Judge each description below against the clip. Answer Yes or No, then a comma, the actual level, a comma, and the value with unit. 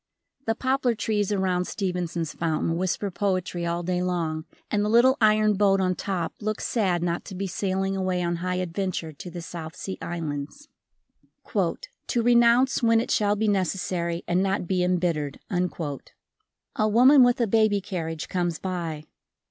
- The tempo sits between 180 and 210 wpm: No, average, 160 wpm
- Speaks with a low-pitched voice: No, medium, 185 Hz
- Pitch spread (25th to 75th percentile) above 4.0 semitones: No, average, 3.6 semitones